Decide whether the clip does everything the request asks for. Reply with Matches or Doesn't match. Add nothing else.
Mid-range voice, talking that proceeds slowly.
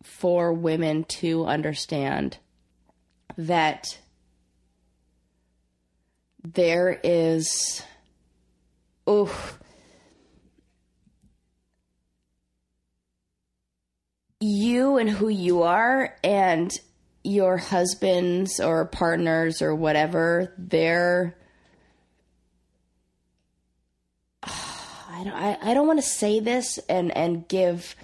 Matches